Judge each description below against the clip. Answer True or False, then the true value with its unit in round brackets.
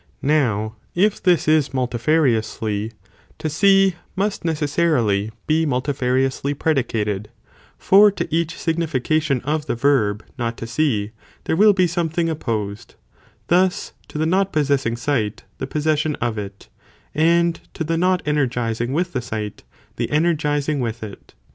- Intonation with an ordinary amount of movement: False (5.9 semitones)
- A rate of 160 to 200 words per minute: False (140 wpm)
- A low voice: False (145 Hz)